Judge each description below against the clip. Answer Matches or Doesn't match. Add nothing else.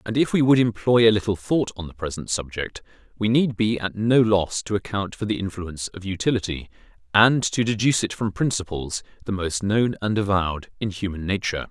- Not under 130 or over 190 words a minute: Doesn't match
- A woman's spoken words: Doesn't match